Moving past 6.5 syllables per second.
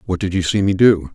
No: 6.0 syllables/s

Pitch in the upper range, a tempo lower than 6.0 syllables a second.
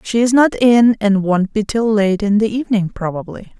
Yes: high, 210 Hz; 5.0 syllables/s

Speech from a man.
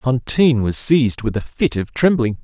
Yes: male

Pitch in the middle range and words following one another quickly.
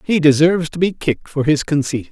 Yes: medium, 155 Hz; fast, 225 wpm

